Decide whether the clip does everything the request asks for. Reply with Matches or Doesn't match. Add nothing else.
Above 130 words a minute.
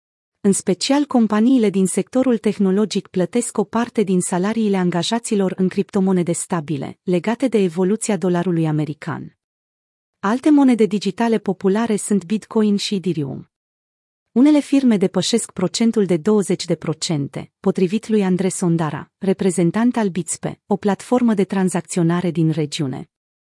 Doesn't match